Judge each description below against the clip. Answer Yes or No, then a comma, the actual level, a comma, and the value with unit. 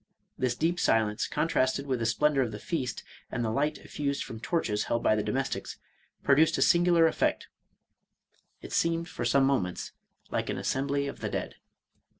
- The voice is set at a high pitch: No, low, 135 Hz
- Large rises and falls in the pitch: No, average, 5.0 semitones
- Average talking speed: Yes, average, 180 wpm